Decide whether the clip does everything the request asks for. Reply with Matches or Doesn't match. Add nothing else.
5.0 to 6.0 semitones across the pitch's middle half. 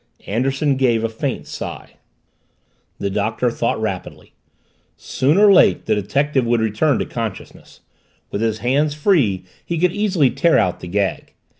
Matches